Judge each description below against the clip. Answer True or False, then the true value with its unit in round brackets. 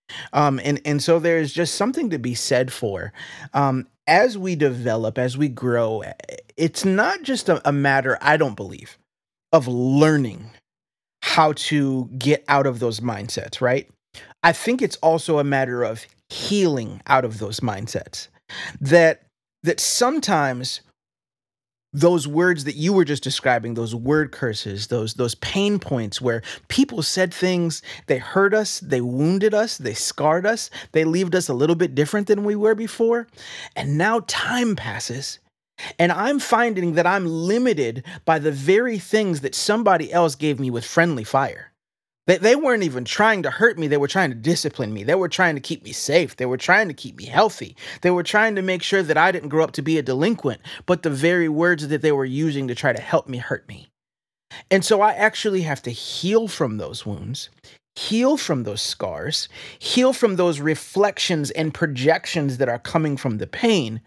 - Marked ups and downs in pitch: True (6.5 semitones)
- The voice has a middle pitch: True (155 Hz)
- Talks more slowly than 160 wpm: False (185 wpm)